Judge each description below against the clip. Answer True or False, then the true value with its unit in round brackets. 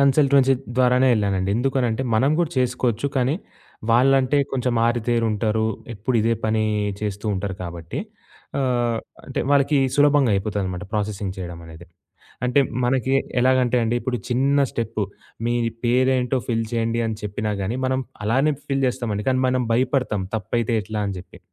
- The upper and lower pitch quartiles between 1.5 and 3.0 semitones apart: False (3.5 semitones)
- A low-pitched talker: True (120 Hz)